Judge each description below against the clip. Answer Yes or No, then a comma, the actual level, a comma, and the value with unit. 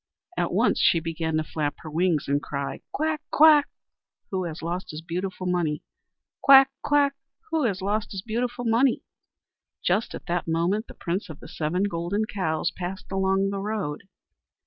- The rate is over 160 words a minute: Yes, average, 170 wpm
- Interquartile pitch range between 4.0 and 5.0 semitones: Yes, average, 4.7 semitones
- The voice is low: No, medium, 185 Hz